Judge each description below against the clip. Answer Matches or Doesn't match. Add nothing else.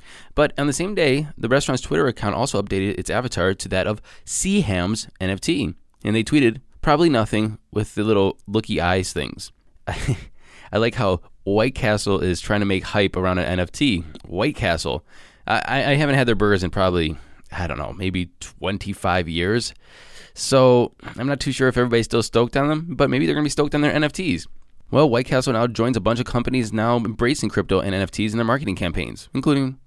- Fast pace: Doesn't match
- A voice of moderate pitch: Doesn't match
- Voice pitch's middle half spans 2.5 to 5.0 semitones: Doesn't match